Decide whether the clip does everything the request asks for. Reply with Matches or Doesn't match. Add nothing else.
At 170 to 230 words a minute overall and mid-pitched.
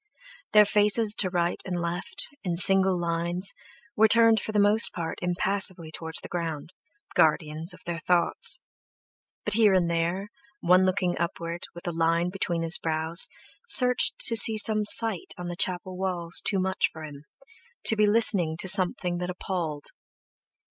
Doesn't match